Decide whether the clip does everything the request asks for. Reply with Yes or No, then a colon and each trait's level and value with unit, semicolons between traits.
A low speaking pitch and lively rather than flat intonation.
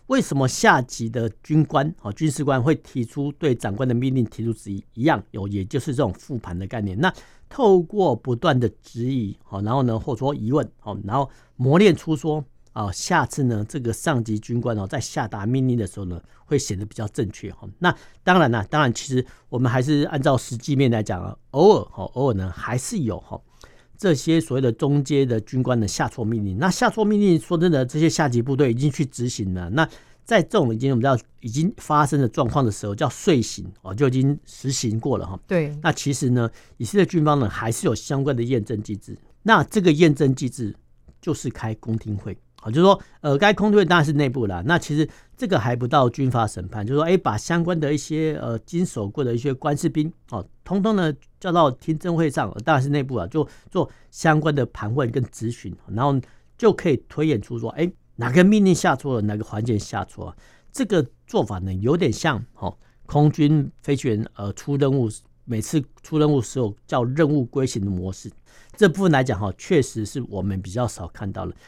Yes: low, 130 Hz; wide, 5.7 semitones